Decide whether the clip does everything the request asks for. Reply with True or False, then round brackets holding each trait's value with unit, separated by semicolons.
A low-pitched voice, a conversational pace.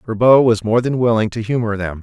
False (115 Hz; 235 wpm)